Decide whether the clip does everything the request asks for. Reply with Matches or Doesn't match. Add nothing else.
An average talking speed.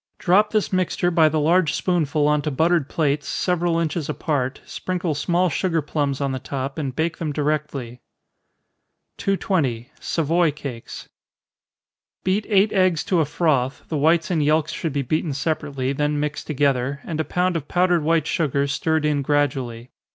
Matches